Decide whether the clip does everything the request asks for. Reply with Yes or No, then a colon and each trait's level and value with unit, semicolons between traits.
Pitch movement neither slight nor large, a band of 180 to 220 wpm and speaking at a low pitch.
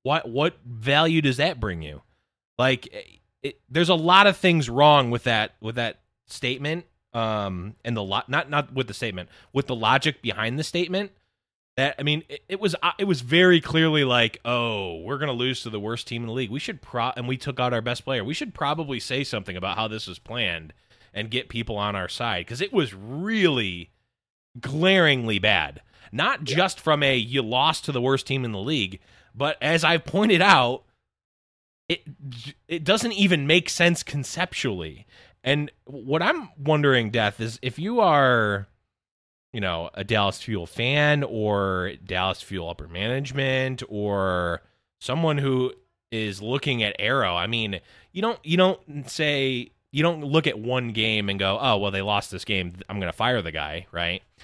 No: wide, 6.1 semitones; average, 185 wpm; low, 125 Hz